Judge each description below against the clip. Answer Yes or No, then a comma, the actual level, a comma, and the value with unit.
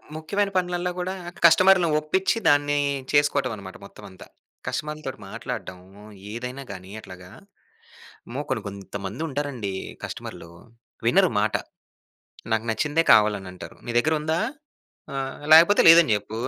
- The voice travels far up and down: Yes, wide, 7.6 semitones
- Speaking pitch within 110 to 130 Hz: No, medium, 140 Hz